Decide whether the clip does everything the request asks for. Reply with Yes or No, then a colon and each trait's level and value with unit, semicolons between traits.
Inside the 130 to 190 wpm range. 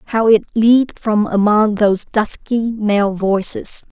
Yes: slow, 135 wpm